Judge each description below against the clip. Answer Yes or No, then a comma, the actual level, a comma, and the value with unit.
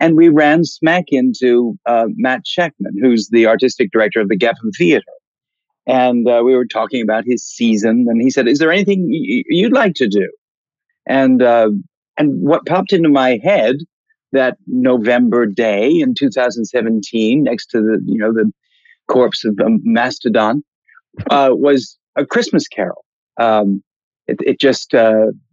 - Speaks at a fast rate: No, average, 160 wpm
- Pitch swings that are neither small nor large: No, wide, 7.9 semitones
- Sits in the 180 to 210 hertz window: No, low, 130 Hz